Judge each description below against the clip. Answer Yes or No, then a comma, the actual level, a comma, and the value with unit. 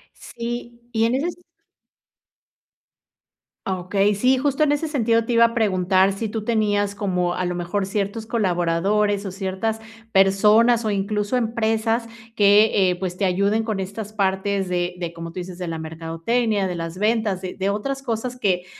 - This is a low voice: No, high, 205 Hz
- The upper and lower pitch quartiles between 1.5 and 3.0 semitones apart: No, average, 3.4 semitones